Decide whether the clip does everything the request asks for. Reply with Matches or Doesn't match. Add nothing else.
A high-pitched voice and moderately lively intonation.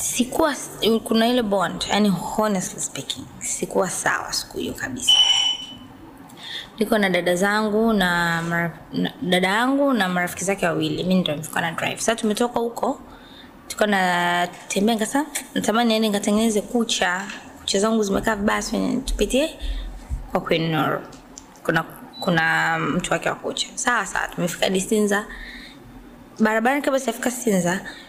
Matches